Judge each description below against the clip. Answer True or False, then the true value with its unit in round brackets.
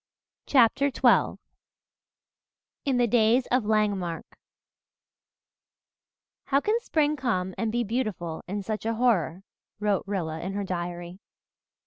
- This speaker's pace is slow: True (115 wpm)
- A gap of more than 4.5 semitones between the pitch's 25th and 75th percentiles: True (5.0 semitones)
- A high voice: True (215 Hz)